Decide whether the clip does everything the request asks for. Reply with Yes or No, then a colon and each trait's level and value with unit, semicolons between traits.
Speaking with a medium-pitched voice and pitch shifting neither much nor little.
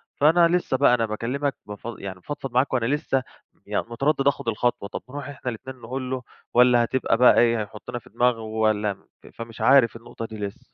No: low, 120 Hz; average, 3.2 semitones